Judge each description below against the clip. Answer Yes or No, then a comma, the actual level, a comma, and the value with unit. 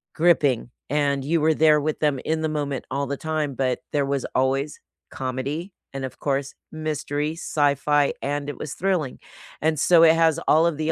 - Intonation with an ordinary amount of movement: No, narrow, 2.2 semitones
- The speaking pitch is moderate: Yes, medium, 150 Hz